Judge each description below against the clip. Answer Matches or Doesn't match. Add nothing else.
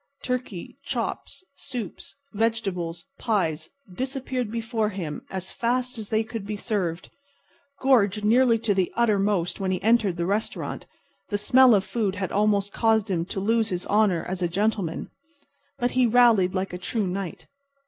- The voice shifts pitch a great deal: Doesn't match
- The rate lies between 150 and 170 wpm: Matches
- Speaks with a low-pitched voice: Doesn't match